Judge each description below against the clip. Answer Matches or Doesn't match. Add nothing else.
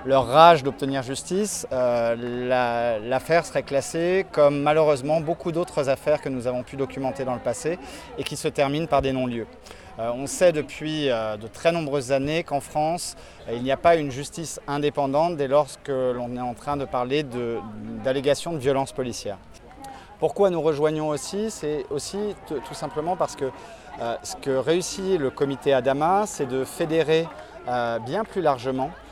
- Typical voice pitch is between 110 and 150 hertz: Matches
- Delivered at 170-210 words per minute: Matches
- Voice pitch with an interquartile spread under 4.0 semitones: Matches